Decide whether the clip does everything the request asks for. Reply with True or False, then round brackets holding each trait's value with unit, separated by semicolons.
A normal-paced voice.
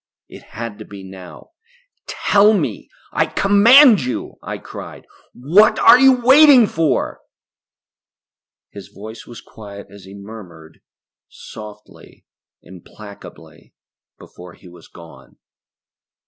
False (110 wpm)